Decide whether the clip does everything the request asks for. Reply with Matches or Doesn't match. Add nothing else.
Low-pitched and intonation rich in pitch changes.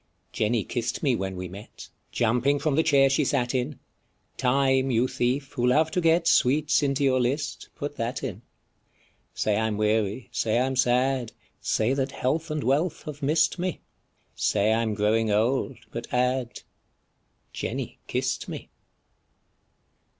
Doesn't match